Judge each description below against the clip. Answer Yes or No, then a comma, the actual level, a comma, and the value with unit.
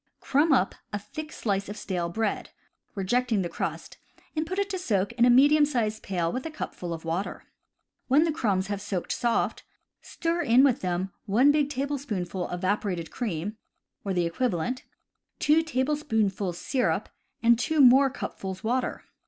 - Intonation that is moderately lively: No, wide, 6.7 semitones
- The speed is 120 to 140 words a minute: No, average, 160 wpm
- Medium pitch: No, high, 230 Hz